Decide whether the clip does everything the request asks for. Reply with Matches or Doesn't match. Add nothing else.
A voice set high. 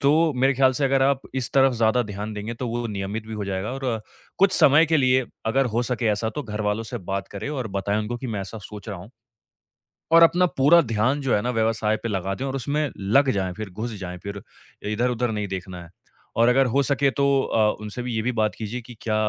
Doesn't match